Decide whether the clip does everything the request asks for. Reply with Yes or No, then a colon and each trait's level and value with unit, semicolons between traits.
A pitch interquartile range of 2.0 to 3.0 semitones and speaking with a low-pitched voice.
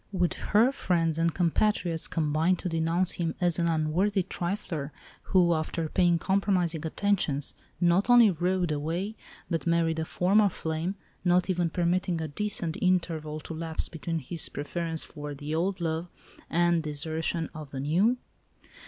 No: narrow, 2.4 semitones; medium, 170 Hz